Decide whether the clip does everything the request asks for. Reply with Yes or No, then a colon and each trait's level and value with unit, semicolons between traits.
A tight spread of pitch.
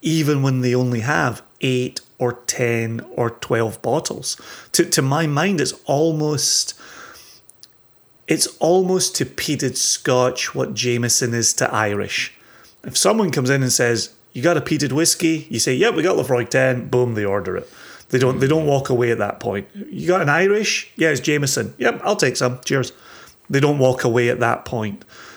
No: average, 4.1 semitones